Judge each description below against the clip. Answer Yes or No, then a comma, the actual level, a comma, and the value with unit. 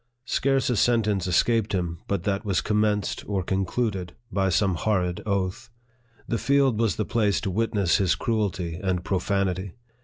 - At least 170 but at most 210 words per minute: No, average, 155 wpm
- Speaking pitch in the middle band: No, low, 100 Hz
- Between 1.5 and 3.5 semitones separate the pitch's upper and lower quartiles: Yes, average, 3.0 semitones